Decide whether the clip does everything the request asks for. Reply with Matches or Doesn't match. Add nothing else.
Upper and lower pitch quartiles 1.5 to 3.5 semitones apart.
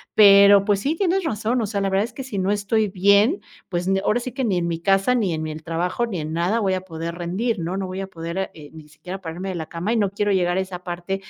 Matches